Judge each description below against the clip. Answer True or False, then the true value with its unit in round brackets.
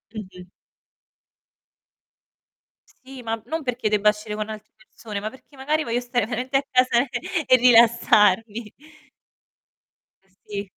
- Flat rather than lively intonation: False (3.1 semitones)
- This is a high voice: True (230 Hz)